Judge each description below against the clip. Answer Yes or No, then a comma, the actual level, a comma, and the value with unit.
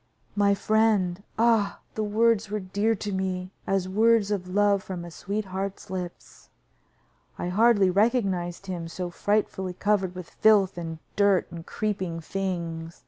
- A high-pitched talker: Yes, high, 195 Hz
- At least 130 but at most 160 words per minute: Yes, average, 150 wpm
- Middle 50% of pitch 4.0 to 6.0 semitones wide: No, narrow, 2.4 semitones